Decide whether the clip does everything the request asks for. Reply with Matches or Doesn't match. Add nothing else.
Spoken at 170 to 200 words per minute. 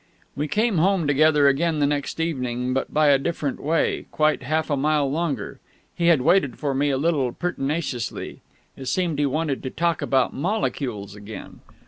Matches